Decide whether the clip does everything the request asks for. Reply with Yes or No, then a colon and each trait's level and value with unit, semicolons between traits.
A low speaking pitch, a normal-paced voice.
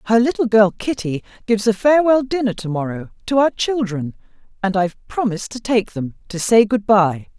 No: high, 215 Hz; average, 185 wpm